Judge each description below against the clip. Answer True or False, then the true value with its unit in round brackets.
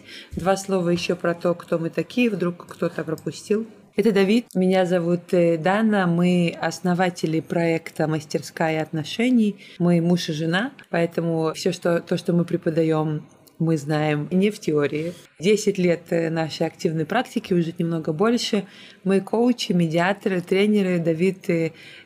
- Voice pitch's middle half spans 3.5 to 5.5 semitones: False (2.9 semitones)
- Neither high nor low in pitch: True (175 Hz)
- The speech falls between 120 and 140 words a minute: True (135 wpm)